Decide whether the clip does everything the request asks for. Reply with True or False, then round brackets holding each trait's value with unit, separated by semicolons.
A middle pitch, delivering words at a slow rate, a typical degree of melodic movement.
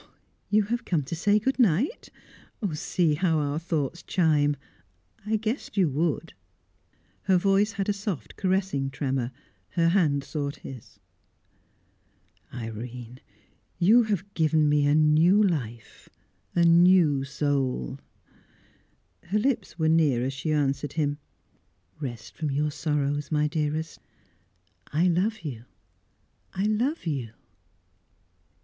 True (155 Hz; 120 wpm; 5.0 semitones)